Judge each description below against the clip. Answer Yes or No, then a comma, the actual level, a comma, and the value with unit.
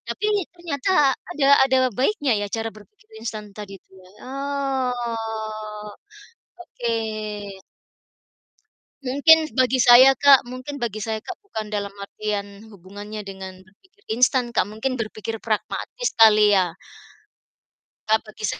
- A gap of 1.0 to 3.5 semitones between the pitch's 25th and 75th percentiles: No, average, 4.2 semitones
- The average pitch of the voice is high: Yes, high, 225 Hz